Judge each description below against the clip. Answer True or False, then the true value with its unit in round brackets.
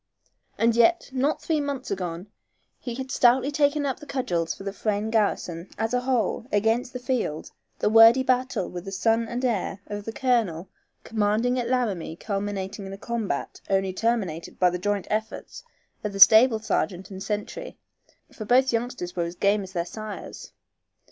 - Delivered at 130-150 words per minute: False (175 wpm)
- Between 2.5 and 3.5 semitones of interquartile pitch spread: False (4.3 semitones)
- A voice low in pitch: False (220 Hz)